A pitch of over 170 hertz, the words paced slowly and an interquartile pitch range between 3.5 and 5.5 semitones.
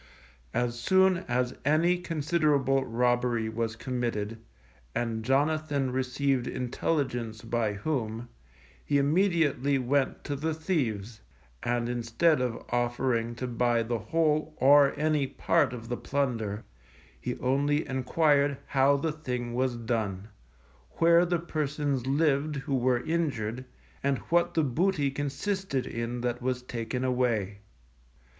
No: low, 130 Hz; slow, 125 wpm; average, 3.8 semitones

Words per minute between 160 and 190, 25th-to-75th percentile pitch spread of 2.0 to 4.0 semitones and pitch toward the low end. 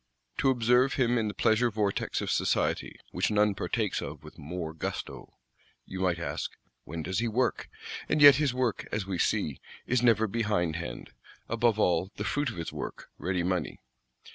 No: average, 175 wpm; wide, 5.5 semitones; low, 105 Hz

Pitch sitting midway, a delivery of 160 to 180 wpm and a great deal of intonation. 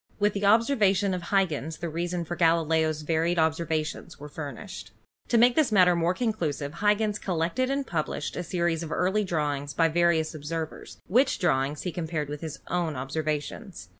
No: medium, 170 Hz; average, 170 wpm; average, 3.7 semitones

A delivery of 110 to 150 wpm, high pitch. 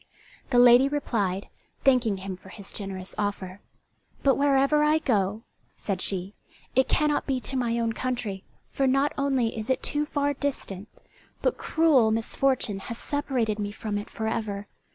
No: average, 160 wpm; high, 235 Hz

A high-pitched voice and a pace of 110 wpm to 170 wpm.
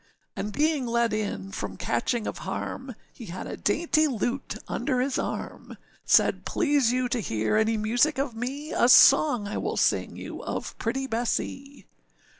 Yes: high, 245 Hz; average, 165 wpm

